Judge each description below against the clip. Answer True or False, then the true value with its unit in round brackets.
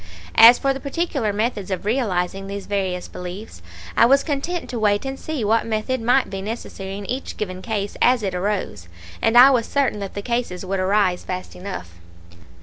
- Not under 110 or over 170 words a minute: False (190 wpm)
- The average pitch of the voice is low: False (210 Hz)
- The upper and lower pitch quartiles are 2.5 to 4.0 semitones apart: False (4.4 semitones)